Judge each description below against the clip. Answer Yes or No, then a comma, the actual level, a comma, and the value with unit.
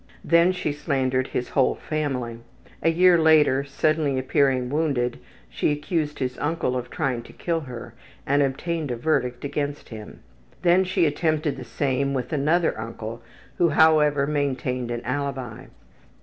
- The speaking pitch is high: No, medium, 140 Hz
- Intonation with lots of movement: No, average, 3.6 semitones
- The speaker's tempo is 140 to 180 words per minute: Yes, average, 150 wpm